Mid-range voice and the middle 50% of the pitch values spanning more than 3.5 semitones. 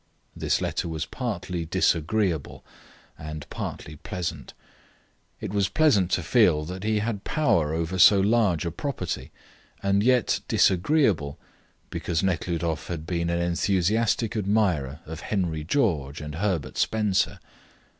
No: very low, 90 Hz; average, 4.6 semitones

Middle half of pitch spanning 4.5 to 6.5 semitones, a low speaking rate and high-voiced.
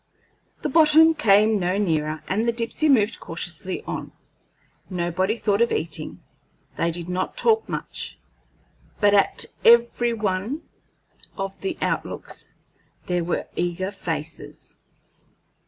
Yes: average, 4.8 semitones; slow, 120 wpm; high, 205 Hz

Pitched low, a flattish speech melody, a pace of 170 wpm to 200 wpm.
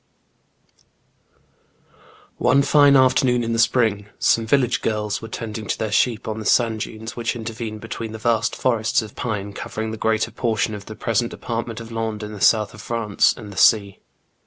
Yes: low, 110 Hz; narrow, 1.5 semitones; average, 180 wpm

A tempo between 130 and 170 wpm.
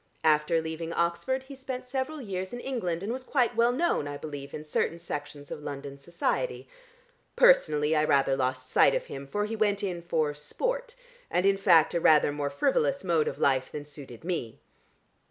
No: average, 190 wpm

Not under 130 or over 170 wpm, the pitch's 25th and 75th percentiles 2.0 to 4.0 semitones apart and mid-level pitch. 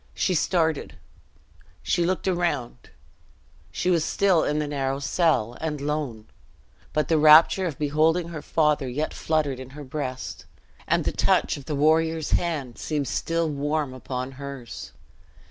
Yes: average, 145 wpm; average, 3.1 semitones; medium, 150 Hz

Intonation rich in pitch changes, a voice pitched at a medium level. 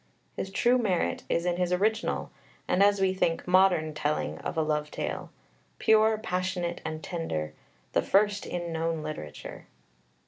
No: average, 3.5 semitones; medium, 180 Hz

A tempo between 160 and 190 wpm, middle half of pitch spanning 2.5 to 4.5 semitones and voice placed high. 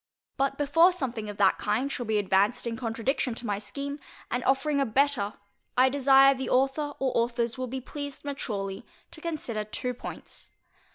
Yes: average, 175 wpm; average, 3.6 semitones; very high, 255 Hz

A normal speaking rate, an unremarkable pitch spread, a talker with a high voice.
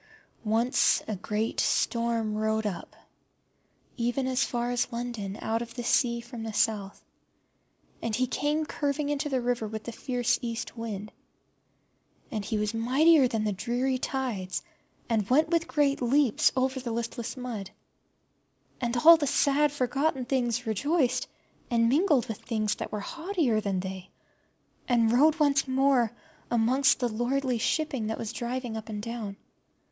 Yes: average, 155 wpm; average, 3.3 semitones; high, 240 Hz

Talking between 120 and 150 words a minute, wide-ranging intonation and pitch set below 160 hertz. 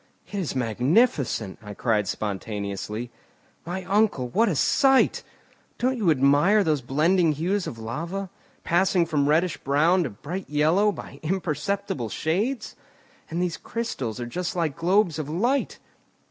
No: average, 140 wpm; wide, 6.5 semitones; medium, 165 Hz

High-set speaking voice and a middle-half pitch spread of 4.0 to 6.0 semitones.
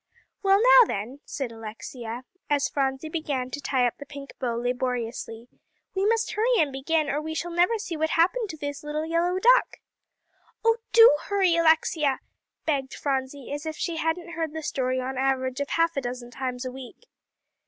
Yes: very high, 290 Hz; average, 4.5 semitones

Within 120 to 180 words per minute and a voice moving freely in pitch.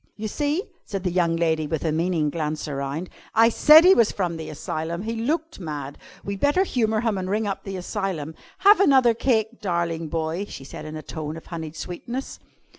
No: average, 200 wpm; wide, 6.2 semitones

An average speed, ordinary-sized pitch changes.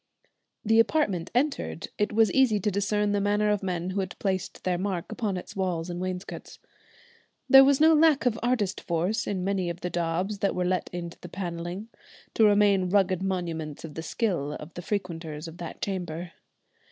Yes: average, 190 wpm; average, 3.1 semitones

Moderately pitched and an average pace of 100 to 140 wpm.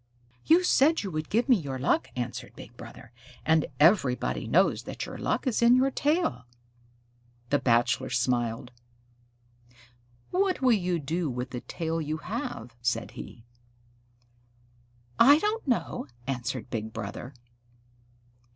Yes: medium, 155 Hz; slow, 135 wpm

